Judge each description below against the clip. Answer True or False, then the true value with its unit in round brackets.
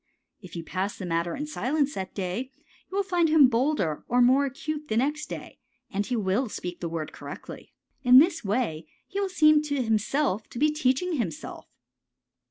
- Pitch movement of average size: False (7.7 semitones)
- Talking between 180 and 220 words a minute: True (185 wpm)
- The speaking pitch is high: True (255 Hz)